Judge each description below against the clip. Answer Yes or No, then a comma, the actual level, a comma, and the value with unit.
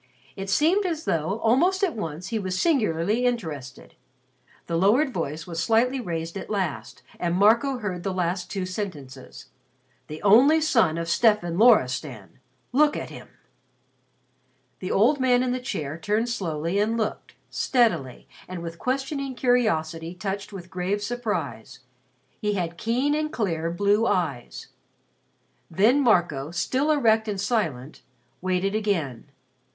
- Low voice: No, high, 200 Hz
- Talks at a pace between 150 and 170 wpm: No, average, 140 wpm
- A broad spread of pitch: Yes, wide, 6.5 semitones